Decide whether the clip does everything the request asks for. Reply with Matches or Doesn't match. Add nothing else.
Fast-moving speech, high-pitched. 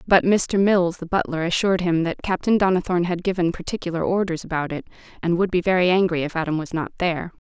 Doesn't match